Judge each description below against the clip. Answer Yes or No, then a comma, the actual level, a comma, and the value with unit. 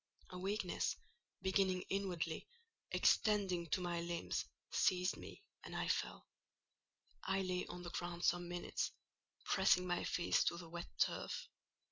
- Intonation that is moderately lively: No, narrow, 1.6 semitones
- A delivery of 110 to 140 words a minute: Yes, slow, 135 wpm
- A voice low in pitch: No, medium, 180 Hz